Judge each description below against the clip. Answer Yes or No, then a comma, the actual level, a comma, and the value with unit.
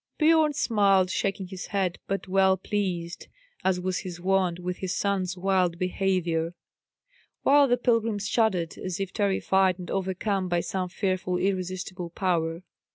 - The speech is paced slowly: No, average, 145 wpm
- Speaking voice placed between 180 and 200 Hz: Yes, high, 190 Hz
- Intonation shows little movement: Yes, narrow, 1.6 semitones